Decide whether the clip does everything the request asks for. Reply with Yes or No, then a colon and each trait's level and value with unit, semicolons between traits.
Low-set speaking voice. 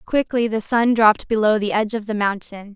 No: high, 215 Hz